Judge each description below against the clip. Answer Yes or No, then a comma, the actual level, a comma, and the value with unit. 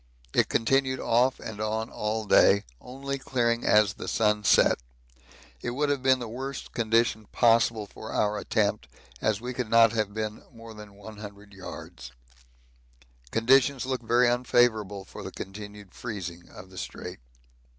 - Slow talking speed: No, average, 150 wpm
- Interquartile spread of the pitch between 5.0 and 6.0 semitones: No, average, 2.9 semitones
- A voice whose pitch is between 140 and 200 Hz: No, low, 110 Hz